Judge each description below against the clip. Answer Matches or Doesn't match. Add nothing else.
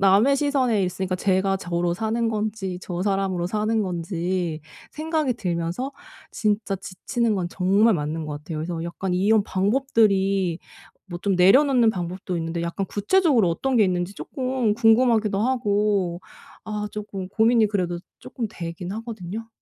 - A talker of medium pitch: Doesn't match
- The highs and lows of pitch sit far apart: Doesn't match